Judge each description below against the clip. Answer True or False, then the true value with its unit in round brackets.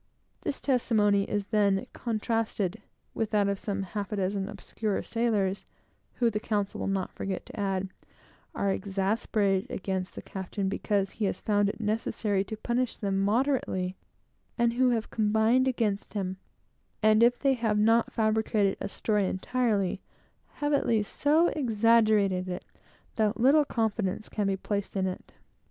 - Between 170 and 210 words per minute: False (150 wpm)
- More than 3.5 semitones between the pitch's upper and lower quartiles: False (2.7 semitones)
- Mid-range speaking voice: False (210 Hz)